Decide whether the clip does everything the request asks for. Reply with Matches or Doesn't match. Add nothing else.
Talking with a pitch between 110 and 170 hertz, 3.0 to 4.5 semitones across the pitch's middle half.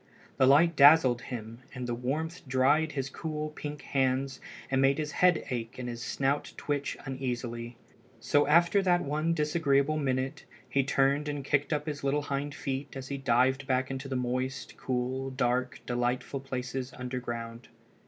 Doesn't match